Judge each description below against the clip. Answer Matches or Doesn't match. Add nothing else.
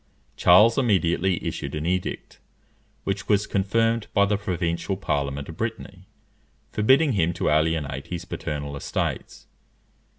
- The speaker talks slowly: Matches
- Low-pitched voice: Matches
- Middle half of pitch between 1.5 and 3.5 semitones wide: Doesn't match